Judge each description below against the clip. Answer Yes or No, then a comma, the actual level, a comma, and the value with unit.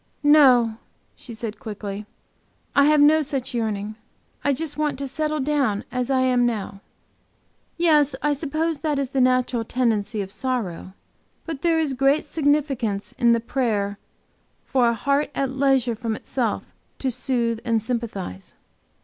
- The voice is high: Yes, very high, 255 Hz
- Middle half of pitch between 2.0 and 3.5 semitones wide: No, average, 4.2 semitones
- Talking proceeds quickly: No, average, 150 wpm